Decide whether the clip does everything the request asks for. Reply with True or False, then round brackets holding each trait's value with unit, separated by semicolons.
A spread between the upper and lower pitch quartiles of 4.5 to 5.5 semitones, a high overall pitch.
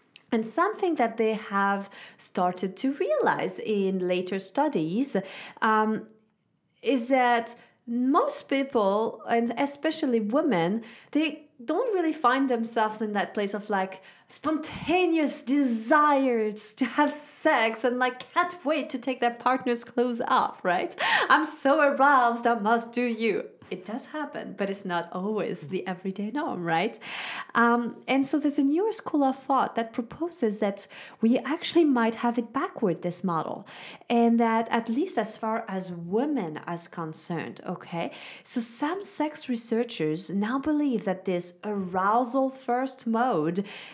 True (5.2 semitones; 235 Hz)